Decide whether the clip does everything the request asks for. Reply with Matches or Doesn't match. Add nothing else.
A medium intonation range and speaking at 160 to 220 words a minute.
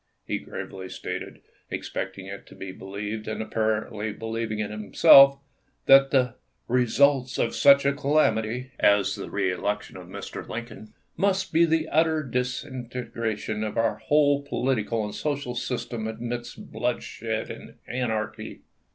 Doesn't match